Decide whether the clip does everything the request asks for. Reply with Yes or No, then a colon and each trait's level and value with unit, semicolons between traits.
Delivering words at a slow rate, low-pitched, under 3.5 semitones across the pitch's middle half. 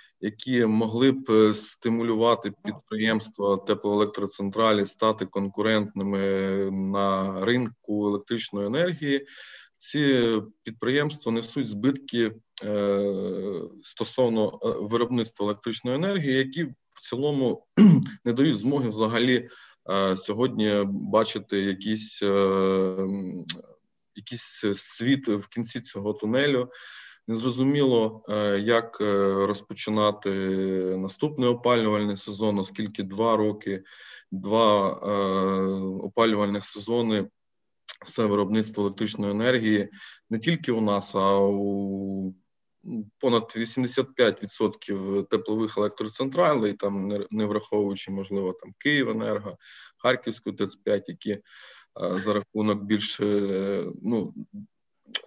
Yes: slow, 85 wpm; low, 105 Hz; average, 2.9 semitones